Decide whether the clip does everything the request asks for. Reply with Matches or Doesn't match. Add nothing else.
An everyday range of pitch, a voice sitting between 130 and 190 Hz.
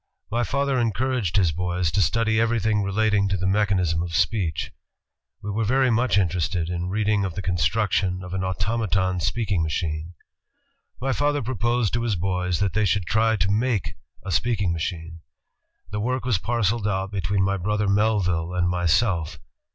Doesn't match